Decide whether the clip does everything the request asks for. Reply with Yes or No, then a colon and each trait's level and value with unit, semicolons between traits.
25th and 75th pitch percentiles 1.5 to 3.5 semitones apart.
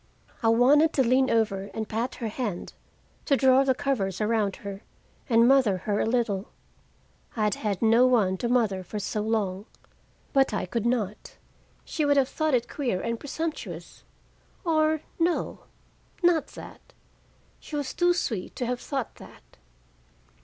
No: average, 4.5 semitones